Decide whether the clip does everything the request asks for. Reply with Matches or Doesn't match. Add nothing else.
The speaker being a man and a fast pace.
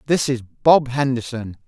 Doesn't match